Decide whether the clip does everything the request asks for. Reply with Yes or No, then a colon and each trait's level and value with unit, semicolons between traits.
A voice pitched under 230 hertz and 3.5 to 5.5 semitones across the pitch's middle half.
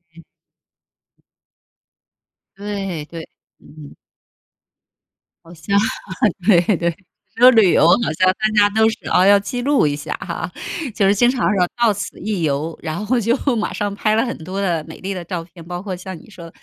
Yes: high, 190 Hz; average, 4.0 semitones